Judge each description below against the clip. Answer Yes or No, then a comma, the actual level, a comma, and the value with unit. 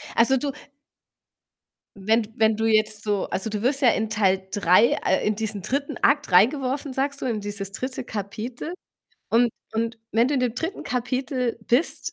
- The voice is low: No, high, 230 Hz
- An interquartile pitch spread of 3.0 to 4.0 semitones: Yes, average, 3.6 semitones